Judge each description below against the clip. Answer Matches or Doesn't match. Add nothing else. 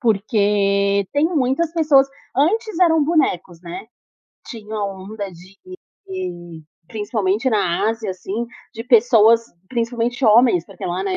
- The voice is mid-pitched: Doesn't match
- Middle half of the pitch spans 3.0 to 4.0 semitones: Doesn't match